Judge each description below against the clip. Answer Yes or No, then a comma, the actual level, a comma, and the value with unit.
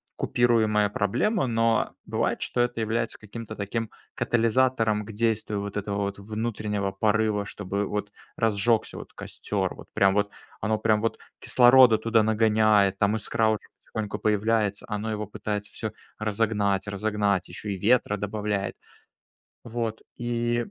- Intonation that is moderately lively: No, narrow, 1.8 semitones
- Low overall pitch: Yes, low, 110 Hz